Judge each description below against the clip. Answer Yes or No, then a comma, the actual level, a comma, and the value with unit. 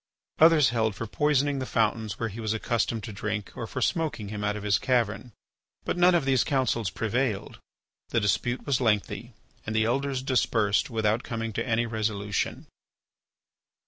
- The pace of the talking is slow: No, average, 170 wpm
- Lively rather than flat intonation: No, average, 3.3 semitones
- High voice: No, low, 115 Hz